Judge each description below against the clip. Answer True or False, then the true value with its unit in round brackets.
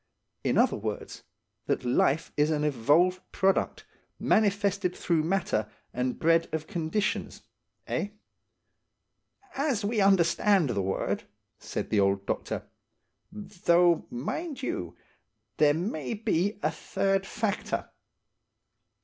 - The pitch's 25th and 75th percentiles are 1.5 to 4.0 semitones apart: False (5.2 semitones)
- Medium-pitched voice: True (175 Hz)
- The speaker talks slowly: True (105 wpm)